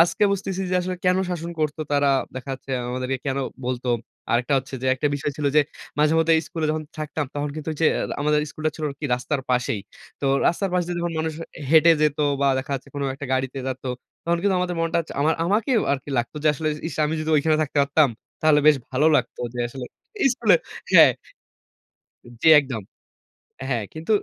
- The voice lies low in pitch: No, medium, 150 Hz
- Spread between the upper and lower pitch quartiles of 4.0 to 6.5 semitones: No, average, 3.2 semitones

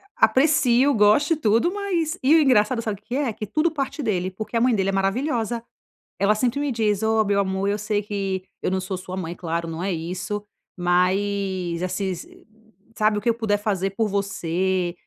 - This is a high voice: Yes, high, 205 Hz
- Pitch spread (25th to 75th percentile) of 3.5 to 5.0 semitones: Yes, average, 4.2 semitones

